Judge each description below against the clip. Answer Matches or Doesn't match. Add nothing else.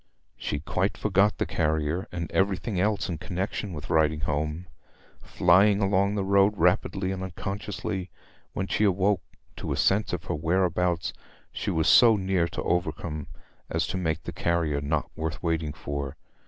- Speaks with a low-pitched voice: Matches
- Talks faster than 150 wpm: Matches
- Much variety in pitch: Doesn't match